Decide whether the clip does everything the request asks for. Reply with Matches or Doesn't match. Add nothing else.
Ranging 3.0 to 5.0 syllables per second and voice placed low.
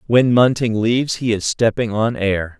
Matches